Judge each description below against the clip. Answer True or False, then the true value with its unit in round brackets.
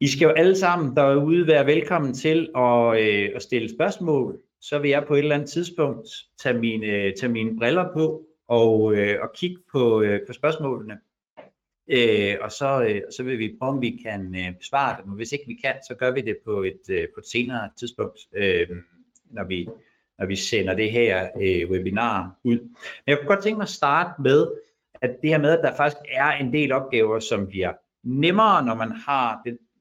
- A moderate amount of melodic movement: False (5.9 semitones)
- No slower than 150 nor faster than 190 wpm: False (205 wpm)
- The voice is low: True (130 Hz)